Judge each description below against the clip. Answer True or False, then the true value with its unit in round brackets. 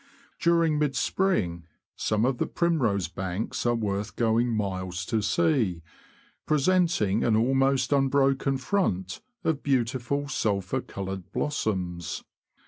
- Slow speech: True (115 wpm)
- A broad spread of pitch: True (6.4 semitones)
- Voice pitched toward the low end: True (120 Hz)